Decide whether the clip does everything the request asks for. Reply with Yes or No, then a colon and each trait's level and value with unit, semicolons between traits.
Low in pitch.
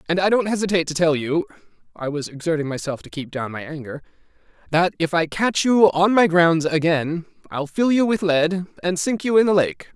No: medium, 170 Hz